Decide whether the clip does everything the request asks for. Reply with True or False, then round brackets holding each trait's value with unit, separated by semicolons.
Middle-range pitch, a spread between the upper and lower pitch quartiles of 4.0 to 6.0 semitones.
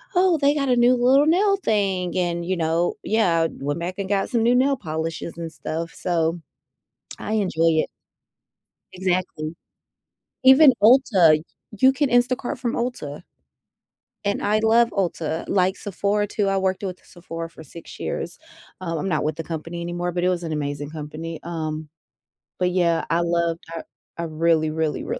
True (175 Hz; 5.1 semitones)